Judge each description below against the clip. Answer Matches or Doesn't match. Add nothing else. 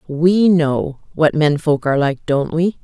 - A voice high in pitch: Doesn't match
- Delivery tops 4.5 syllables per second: Doesn't match